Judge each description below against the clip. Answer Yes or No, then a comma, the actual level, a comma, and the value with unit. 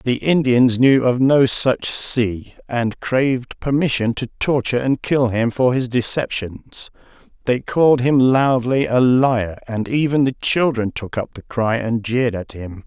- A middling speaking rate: Yes, average, 170 wpm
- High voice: No, low, 125 Hz